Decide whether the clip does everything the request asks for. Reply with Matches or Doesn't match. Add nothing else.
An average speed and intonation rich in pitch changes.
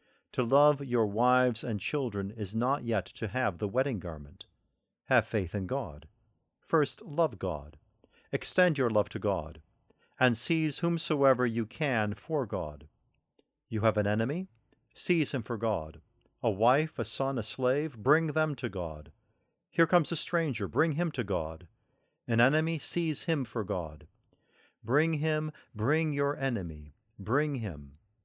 Matches